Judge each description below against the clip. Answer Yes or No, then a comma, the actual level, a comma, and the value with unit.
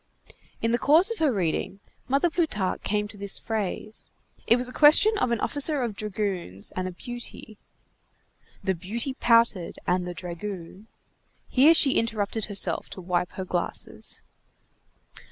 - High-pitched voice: Yes, high, 215 Hz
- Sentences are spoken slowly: No, average, 150 wpm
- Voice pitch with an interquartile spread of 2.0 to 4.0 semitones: No, average, 5.3 semitones